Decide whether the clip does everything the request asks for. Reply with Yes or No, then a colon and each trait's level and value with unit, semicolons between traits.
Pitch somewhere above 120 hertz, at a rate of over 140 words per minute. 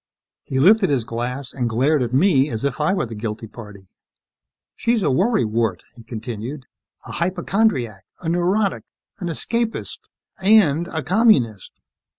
Yes: medium, 140 Hz; average, 150 wpm